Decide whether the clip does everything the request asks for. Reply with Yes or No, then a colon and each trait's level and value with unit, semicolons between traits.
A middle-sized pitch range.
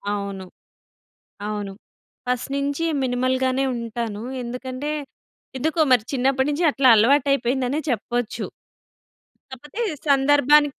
Yes: average, 3.0 semitones